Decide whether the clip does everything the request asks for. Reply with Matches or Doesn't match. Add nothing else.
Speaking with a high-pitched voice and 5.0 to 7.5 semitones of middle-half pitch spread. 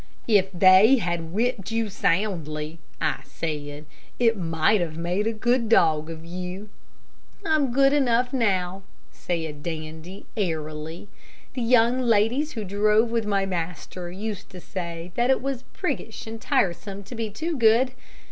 Matches